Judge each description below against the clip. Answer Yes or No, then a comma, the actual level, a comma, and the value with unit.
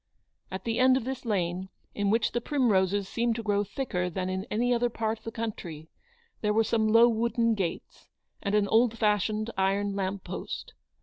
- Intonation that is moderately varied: Yes, average, 3.1 semitones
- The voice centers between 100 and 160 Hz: No, high, 215 Hz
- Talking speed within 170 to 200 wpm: Yes, average, 190 wpm